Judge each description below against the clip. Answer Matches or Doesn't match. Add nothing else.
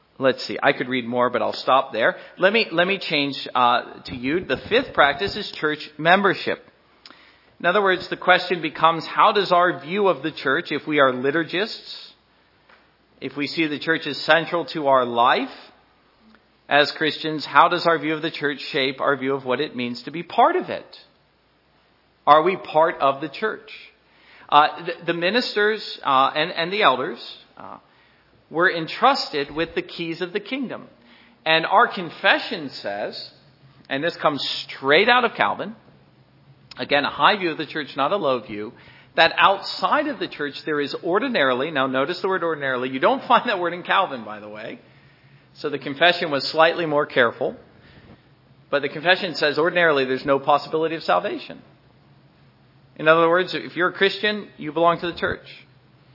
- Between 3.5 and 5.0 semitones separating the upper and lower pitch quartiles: Matches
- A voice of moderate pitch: Matches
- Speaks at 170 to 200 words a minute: Matches